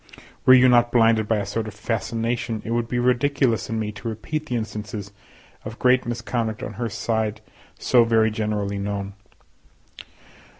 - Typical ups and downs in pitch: No, narrow, 2.0 semitones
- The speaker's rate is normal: Yes, average, 165 wpm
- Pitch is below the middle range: Yes, low, 115 Hz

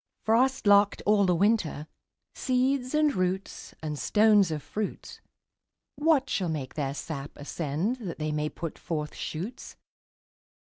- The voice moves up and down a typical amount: No, wide, 7.0 semitones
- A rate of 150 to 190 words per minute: No, slow, 135 wpm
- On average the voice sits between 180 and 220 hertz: Yes, high, 190 Hz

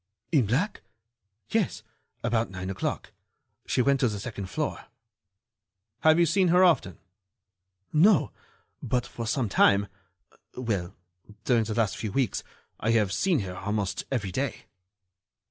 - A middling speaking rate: No, slow, 130 wpm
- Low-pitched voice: Yes, low, 115 Hz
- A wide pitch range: Yes, wide, 5.9 semitones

